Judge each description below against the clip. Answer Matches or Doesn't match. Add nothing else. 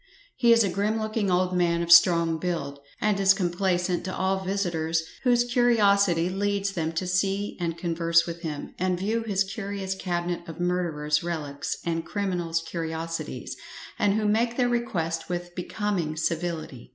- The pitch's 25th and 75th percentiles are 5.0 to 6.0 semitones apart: Doesn't match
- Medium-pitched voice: Matches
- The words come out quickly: Doesn't match